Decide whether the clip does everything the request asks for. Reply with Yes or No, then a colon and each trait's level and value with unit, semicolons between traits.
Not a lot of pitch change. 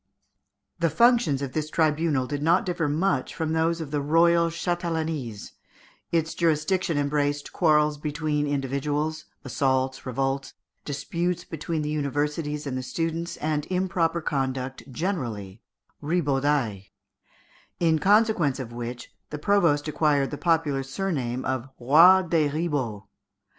No: average, 3.4 semitones